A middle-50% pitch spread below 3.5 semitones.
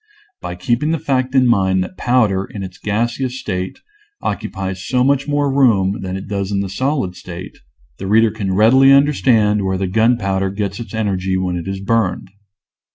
No: average, 4.7 semitones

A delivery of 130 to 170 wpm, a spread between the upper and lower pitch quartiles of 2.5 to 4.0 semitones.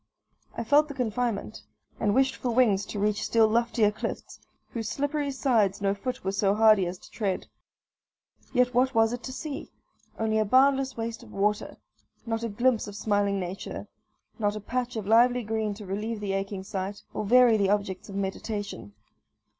No: average, 180 wpm; average, 3.4 semitones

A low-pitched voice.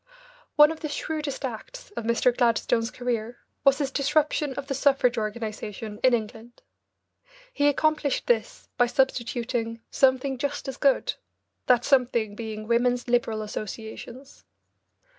No: high, 245 Hz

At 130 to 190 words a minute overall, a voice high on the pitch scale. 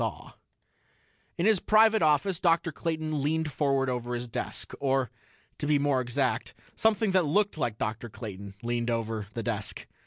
No: average, 155 wpm; medium, 140 Hz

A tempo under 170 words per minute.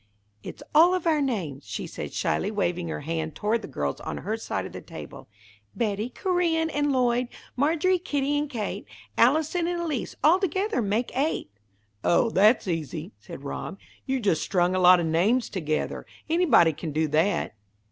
No: average, 175 wpm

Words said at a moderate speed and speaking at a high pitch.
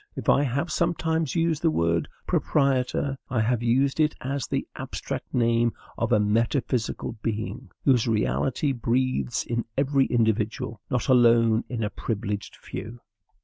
No: average, 145 wpm; low, 120 Hz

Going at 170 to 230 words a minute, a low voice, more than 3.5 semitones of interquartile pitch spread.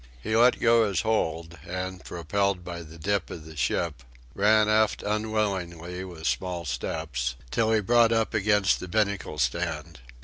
No: average, 160 wpm; very low, 95 Hz; average, 4.4 semitones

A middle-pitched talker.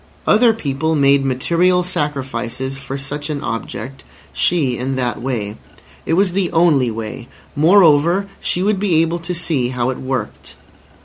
Yes: medium, 145 Hz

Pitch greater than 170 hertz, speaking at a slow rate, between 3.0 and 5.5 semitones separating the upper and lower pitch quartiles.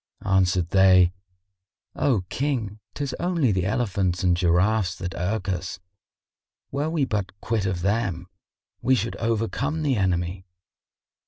No: low, 100 Hz; slow, 130 wpm; average, 4.3 semitones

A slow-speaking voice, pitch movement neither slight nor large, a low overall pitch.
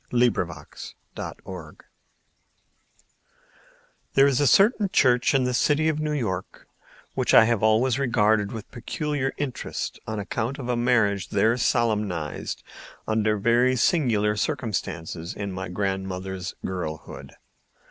Yes: slow, 125 wpm; average, 4.8 semitones; low, 110 Hz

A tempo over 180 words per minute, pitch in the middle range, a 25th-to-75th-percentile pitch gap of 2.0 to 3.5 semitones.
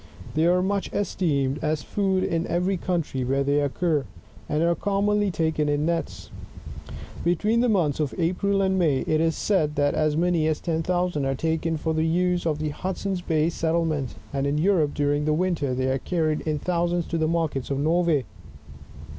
Yes: average, 190 wpm; medium, 160 Hz; average, 3.1 semitones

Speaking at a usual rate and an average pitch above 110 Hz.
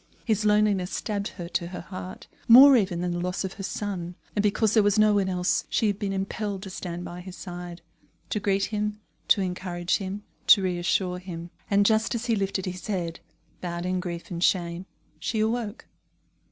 Yes: average, 195 wpm; high, 190 Hz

